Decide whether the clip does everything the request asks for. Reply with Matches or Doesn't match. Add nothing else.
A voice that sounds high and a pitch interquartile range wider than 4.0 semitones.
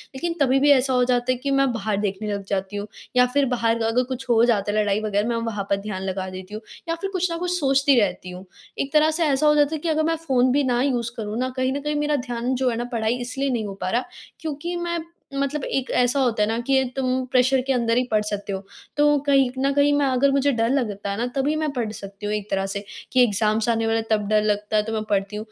Matches